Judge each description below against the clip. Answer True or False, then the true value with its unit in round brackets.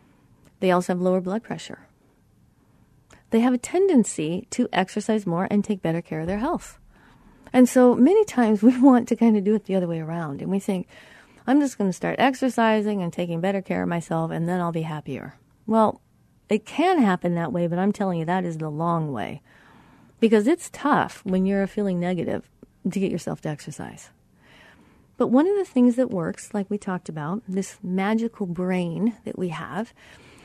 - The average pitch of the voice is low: False (195 Hz)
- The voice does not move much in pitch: False (4.6 semitones)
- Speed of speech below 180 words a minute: False (195 wpm)